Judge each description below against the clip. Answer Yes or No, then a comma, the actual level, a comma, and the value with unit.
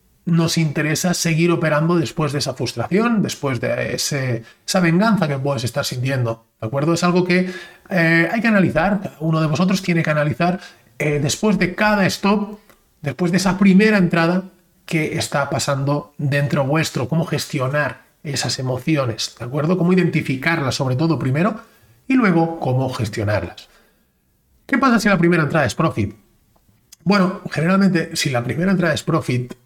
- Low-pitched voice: No, medium, 165 Hz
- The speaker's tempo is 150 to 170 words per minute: Yes, average, 160 wpm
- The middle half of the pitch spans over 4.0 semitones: Yes, average, 4.4 semitones